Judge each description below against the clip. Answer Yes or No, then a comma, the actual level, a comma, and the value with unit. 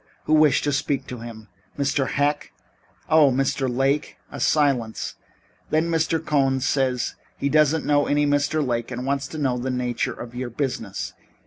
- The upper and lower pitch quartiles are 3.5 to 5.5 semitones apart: No, average, 2.7 semitones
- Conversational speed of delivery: Yes, average, 165 wpm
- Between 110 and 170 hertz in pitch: Yes, medium, 140 Hz